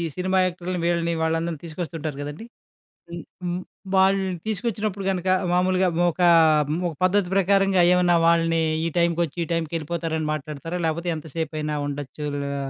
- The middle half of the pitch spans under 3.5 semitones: Yes, narrow, 2.4 semitones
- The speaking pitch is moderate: Yes, medium, 170 Hz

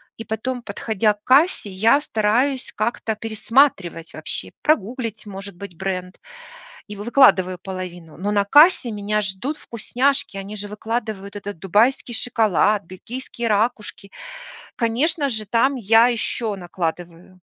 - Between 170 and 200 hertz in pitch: No, high, 215 Hz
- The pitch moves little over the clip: No, average, 3.6 semitones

